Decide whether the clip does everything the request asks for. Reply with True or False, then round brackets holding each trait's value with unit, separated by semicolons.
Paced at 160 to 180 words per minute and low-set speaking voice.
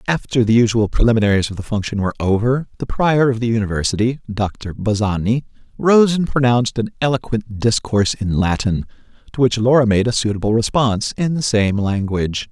True (170 wpm; 115 Hz)